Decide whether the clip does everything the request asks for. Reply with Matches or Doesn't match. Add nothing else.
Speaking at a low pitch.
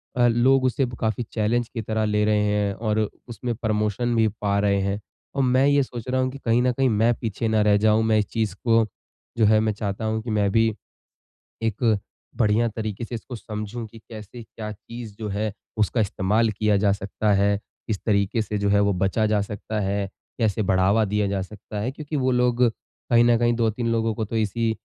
Matches